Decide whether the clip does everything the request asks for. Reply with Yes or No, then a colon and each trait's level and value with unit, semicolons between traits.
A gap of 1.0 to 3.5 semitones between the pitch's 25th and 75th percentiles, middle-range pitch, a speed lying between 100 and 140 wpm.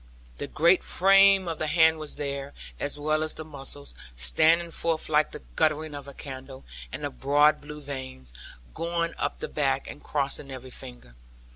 No: average, 2.9 semitones; medium, 150 Hz; average, 175 wpm